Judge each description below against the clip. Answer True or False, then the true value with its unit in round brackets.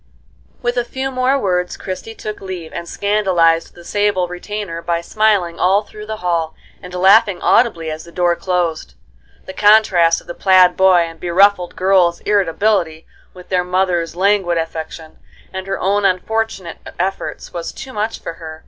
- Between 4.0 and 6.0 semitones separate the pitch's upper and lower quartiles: False (3.2 semitones)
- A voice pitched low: False (185 Hz)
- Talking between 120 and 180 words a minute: True (165 wpm)